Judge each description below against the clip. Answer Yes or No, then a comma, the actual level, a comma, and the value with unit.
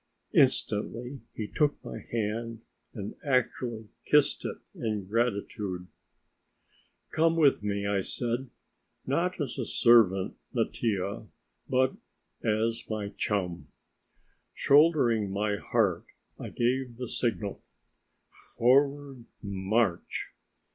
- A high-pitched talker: No, low, 115 Hz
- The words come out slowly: Yes, slow, 100 wpm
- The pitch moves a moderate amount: Yes, average, 4.2 semitones